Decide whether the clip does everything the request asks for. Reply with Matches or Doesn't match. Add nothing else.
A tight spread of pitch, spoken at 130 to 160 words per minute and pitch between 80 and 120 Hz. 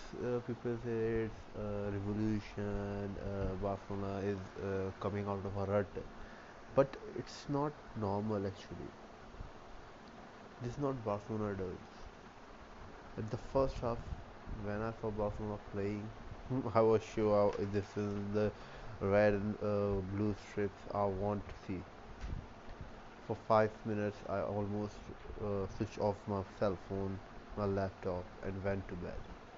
Matches